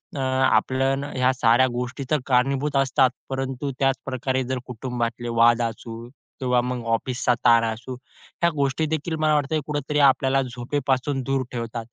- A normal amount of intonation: No, narrow, 2.0 semitones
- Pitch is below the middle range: Yes, low, 130 Hz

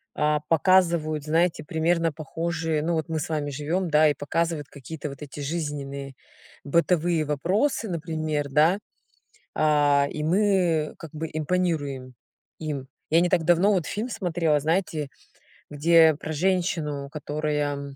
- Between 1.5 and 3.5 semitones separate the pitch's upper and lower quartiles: Yes, narrow, 2.4 semitones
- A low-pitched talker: No, medium, 155 Hz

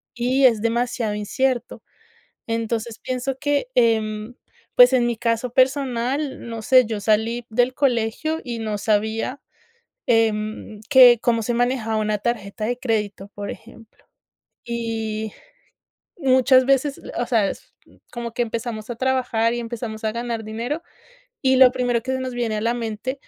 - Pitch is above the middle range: Yes, high, 235 Hz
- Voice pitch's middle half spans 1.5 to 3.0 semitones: Yes, narrow, 2.5 semitones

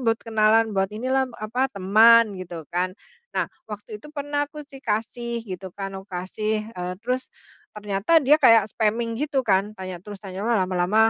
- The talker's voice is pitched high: Yes, high, 215 Hz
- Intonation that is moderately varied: Yes, average, 3.6 semitones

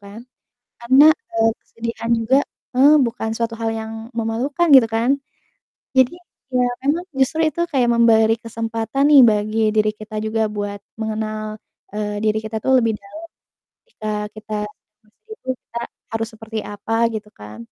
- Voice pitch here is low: No, high, 225 Hz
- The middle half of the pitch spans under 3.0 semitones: Yes, narrow, 2.6 semitones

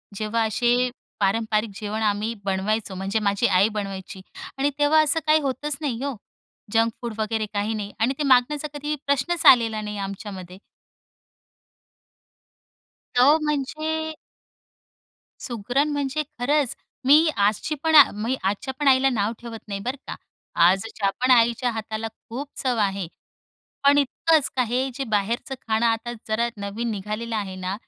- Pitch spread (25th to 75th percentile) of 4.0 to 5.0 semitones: Yes, average, 4.4 semitones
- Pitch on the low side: No, high, 230 Hz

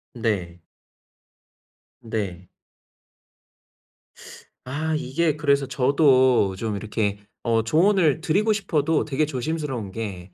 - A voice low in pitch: Yes, low, 130 Hz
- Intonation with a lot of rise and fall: Yes, wide, 6.3 semitones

